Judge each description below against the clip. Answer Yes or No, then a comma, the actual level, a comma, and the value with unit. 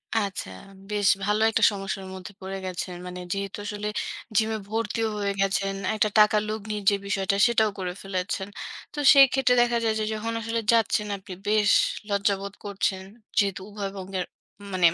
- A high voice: Yes, high, 205 Hz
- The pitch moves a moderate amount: No, narrow, 2.0 semitones